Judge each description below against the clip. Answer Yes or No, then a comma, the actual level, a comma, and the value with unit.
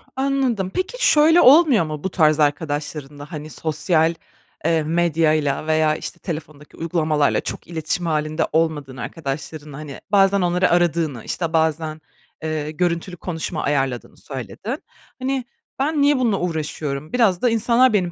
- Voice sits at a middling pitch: Yes, medium, 160 Hz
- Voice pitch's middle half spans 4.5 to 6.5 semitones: No, average, 4.1 semitones